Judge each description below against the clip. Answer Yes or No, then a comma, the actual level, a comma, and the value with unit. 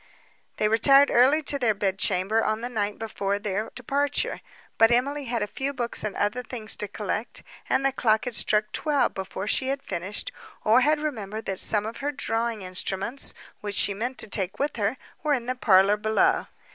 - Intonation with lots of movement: No, average, 4.4 semitones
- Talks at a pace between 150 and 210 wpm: Yes, average, 195 wpm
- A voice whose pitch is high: Yes, high, 225 Hz